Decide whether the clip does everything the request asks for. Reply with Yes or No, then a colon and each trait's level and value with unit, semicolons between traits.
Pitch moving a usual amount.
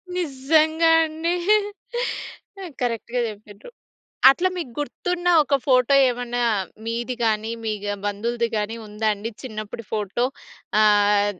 Yes: average, 4.7 semitones